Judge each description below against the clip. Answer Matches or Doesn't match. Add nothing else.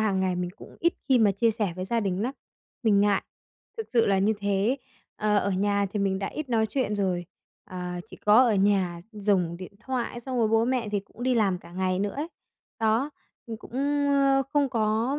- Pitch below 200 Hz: Doesn't match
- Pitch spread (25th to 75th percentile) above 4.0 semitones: Doesn't match